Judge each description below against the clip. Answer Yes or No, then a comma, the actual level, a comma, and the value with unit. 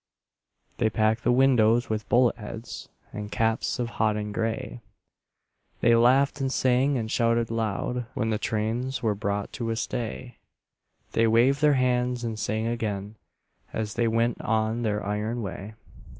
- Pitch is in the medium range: No, low, 115 Hz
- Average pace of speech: Yes, average, 150 wpm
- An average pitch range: No, narrow, 2.1 semitones